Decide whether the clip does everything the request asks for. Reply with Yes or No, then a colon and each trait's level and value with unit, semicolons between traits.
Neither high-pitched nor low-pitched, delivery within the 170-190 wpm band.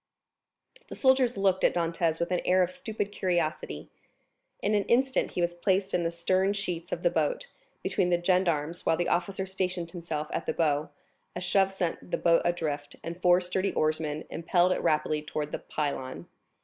Yes: medium, 175 Hz; average, 185 wpm